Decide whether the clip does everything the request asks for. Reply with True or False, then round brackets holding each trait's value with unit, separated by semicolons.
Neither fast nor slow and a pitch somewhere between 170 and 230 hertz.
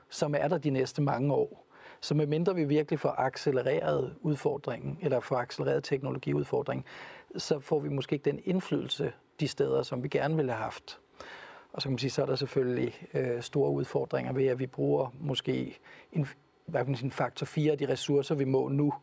False (185 wpm; 145 Hz)